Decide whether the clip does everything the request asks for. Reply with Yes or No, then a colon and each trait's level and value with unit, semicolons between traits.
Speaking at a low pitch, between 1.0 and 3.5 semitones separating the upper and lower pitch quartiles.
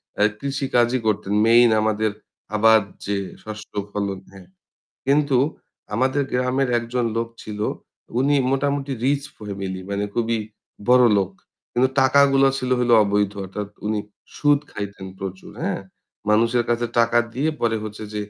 No: low, 115 Hz; average, 4.1 semitones